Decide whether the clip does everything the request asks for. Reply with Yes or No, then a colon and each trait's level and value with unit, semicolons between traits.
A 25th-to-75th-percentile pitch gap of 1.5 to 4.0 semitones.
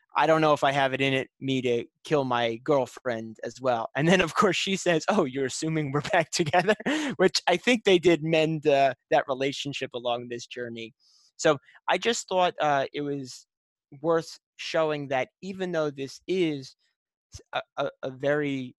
No: average, 4.7 semitones